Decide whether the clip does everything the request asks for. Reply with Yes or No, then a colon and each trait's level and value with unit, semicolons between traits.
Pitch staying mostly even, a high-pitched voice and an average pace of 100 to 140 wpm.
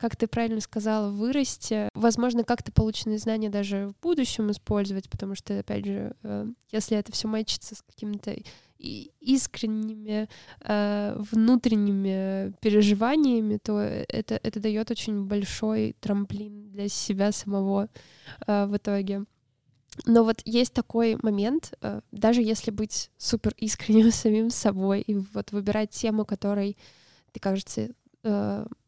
Yes: narrow, 1.8 semitones; high, 215 Hz; average, 120 wpm